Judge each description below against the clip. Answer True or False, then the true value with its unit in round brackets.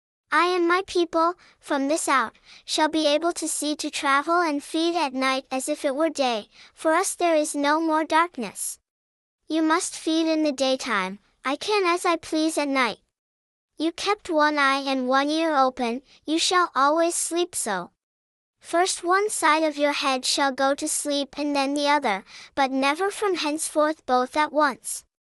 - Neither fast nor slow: True (185 wpm)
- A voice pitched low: False (300 Hz)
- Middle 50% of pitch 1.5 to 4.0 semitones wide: True (3.2 semitones)